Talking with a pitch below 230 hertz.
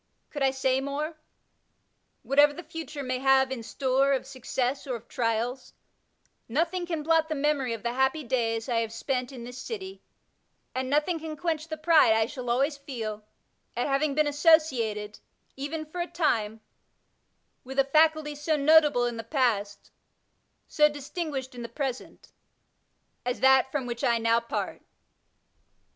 No: very high, 270 Hz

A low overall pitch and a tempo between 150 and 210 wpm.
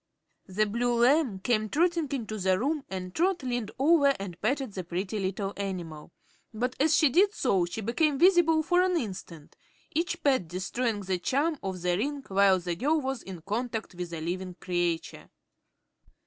No: high, 220 Hz; average, 175 wpm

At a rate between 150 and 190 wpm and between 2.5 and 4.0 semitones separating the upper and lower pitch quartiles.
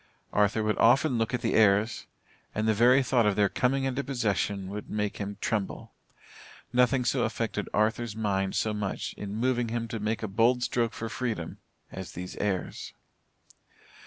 Yes: average, 170 wpm; average, 2.9 semitones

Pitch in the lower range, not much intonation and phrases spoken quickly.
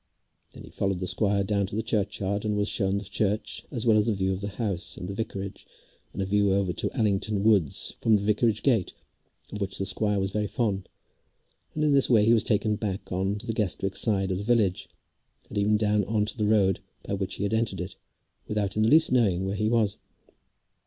Yes: low, 105 Hz; narrow, 1.9 semitones; fast, 230 wpm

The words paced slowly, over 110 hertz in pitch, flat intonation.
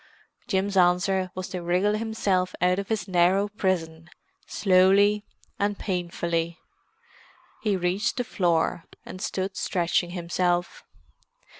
Yes: slow, 115 wpm; medium, 185 Hz; narrow, 2.3 semitones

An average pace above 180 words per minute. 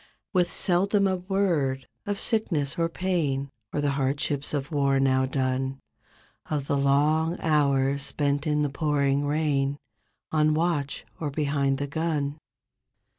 No: slow, 135 wpm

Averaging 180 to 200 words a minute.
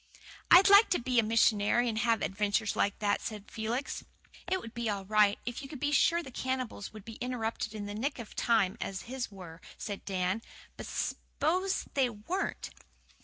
Yes: average, 190 wpm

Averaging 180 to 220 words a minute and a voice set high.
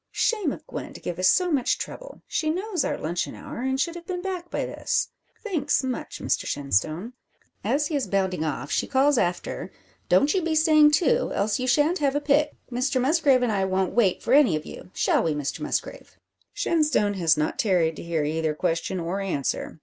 Yes: fast, 205 wpm; very high, 255 Hz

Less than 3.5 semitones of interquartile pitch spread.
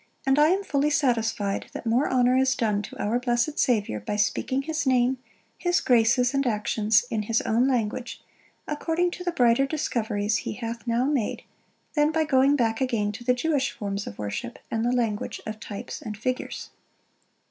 No: average, 4.0 semitones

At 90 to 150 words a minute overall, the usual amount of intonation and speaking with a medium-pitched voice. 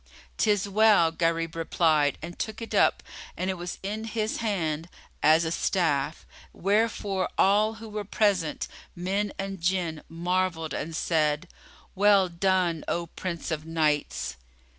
Yes: average, 140 wpm; average, 3.7 semitones; medium, 180 Hz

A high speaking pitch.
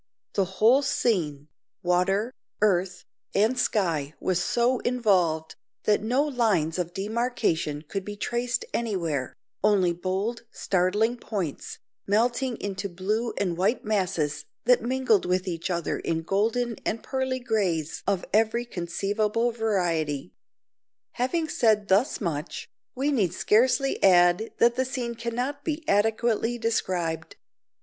Yes: high, 210 Hz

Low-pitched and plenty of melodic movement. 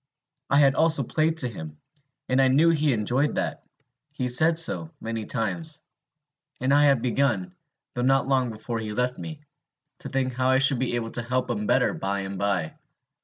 No: low, 130 Hz; average, 3.9 semitones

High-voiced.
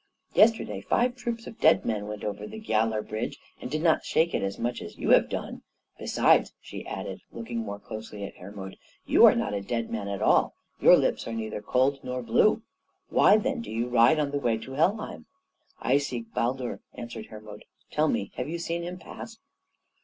No: low, 120 Hz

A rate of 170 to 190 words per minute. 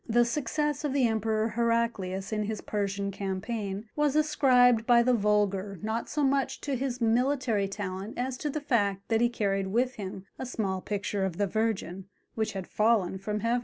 Yes: average, 185 wpm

